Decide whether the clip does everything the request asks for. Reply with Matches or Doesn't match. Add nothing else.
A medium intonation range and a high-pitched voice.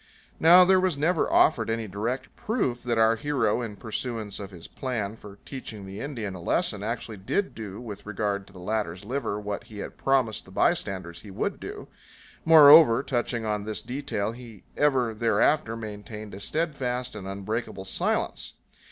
Doesn't match